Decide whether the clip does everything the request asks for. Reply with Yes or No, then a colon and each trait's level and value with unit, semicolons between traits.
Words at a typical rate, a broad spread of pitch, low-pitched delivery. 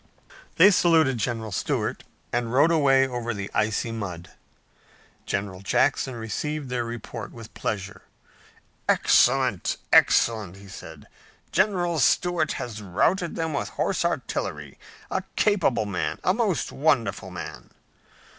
No: slow, 120 wpm; wide, 7.0 semitones; low, 120 Hz